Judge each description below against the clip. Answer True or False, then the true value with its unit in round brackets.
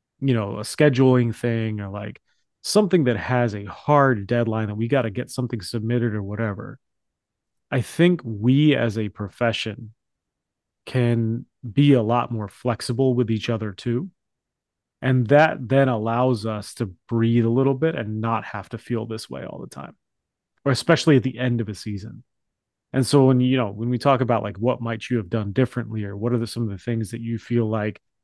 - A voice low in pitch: True (120 Hz)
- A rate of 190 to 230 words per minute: True (200 wpm)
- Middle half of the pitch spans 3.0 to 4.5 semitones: False (2.6 semitones)